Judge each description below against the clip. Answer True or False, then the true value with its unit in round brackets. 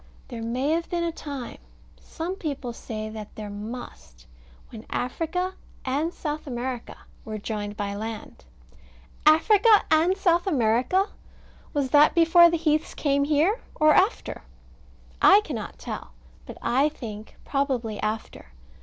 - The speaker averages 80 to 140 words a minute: True (135 wpm)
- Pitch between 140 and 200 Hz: False (280 Hz)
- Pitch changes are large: True (6.7 semitones)